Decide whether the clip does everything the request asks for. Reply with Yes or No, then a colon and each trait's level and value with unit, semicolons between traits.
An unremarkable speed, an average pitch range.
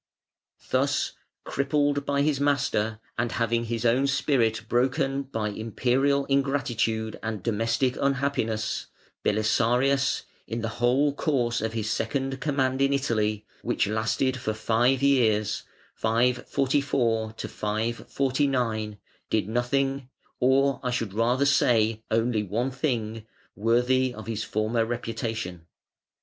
No: slow, 115 wpm; average, 3.6 semitones